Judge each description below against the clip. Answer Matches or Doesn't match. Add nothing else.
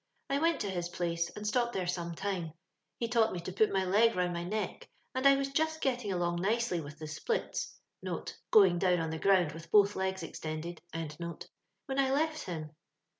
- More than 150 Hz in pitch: Matches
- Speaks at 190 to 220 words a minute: Matches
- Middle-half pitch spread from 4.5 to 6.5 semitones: Matches